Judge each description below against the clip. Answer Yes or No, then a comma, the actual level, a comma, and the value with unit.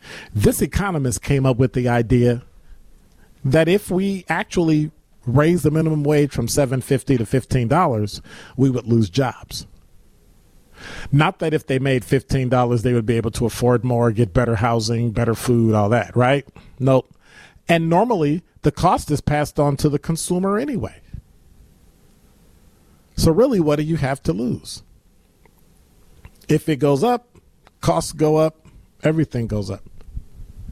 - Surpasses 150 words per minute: No, average, 145 wpm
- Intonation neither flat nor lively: Yes, average, 4.6 semitones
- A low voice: Yes, low, 130 Hz